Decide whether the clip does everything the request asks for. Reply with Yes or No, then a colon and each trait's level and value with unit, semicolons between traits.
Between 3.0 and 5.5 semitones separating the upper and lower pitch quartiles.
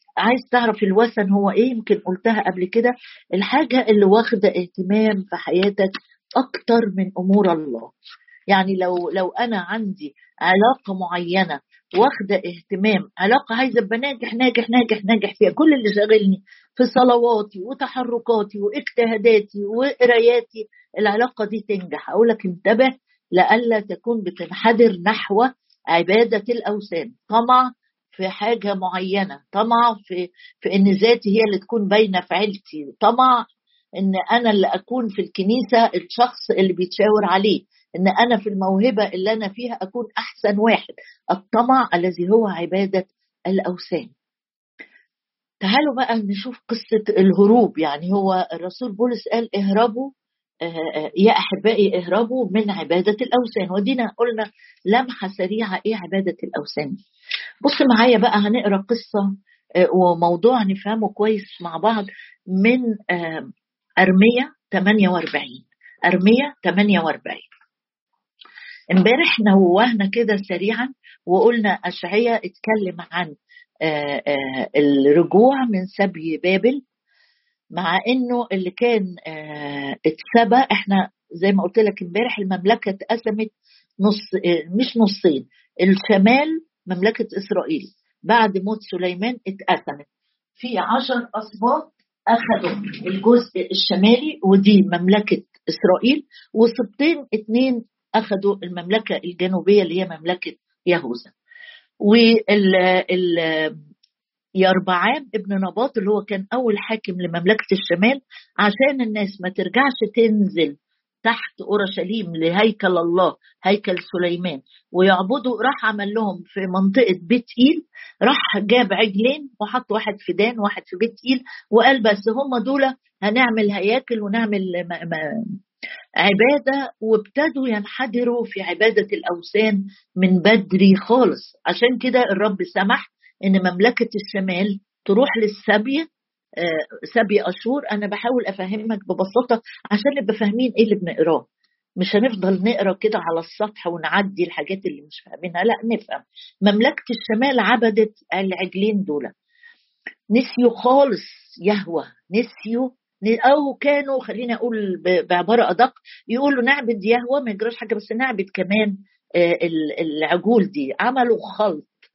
Yes: average, 4.1 semitones